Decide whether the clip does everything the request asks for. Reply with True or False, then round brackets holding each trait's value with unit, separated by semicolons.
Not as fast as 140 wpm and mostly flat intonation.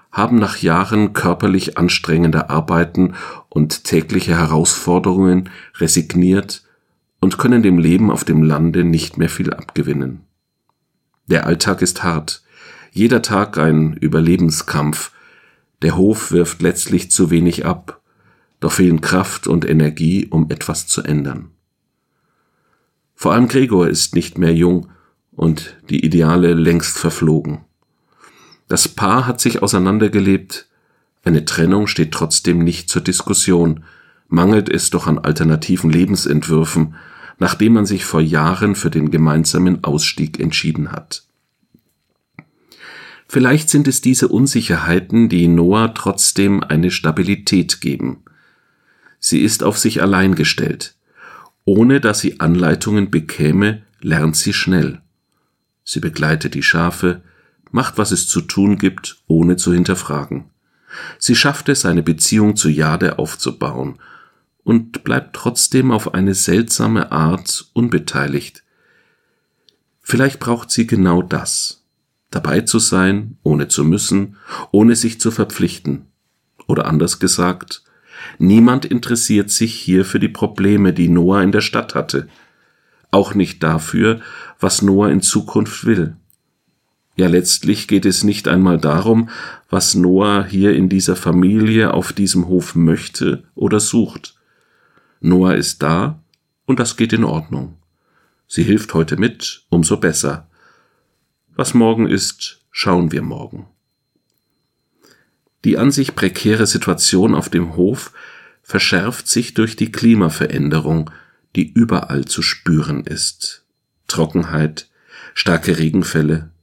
False (125 wpm; 4.2 semitones)